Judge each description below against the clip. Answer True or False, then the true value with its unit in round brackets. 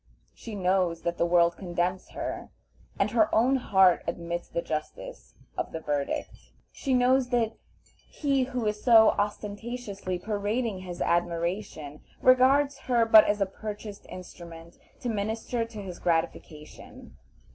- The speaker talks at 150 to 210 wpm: False (135 wpm)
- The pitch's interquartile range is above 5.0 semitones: True (5.4 semitones)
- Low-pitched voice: False (205 Hz)